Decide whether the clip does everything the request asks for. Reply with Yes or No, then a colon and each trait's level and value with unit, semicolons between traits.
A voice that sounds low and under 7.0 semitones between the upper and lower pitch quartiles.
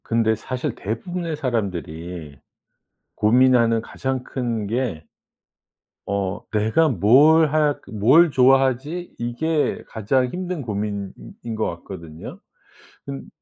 Yes: low, 120 Hz; average, 5.2 semitones